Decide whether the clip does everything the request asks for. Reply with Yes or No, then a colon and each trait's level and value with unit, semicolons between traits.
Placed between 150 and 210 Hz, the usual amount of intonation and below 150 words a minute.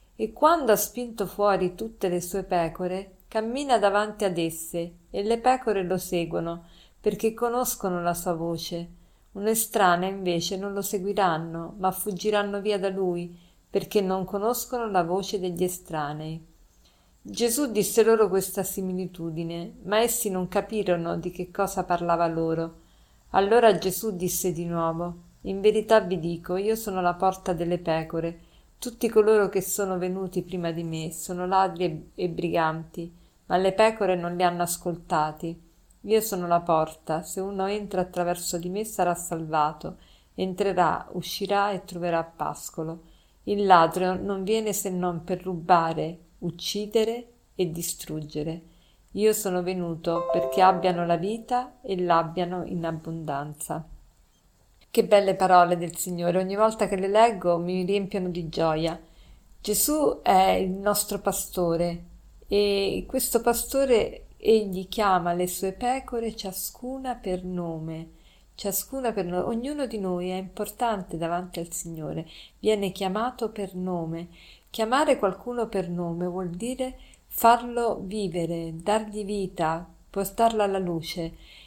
Yes: medium, 185 Hz; average, 3.3 semitones; average, 135 wpm